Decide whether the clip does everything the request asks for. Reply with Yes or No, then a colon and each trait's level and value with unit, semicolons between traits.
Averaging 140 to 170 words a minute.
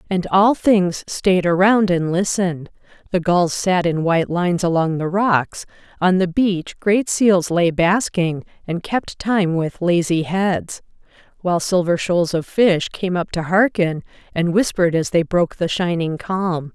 Yes: average, 165 wpm